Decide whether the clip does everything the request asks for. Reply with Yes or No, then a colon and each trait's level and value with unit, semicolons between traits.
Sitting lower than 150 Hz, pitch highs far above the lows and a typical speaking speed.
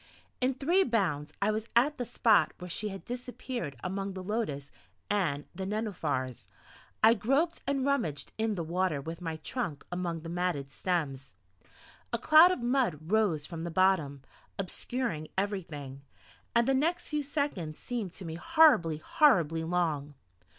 No: high, 190 Hz; wide, 7.2 semitones; average, 155 wpm